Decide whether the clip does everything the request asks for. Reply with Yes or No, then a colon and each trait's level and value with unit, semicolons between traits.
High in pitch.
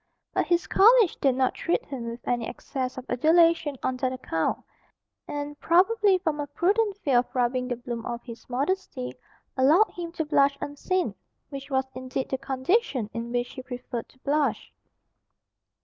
Yes: very high, 270 Hz